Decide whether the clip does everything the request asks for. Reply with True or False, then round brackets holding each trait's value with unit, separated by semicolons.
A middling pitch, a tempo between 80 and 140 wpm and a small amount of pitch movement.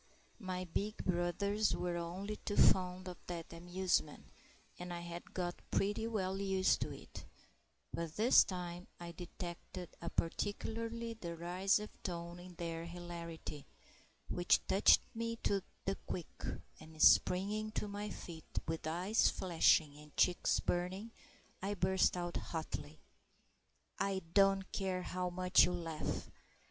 True (180 Hz; 135 wpm; 2.3 semitones)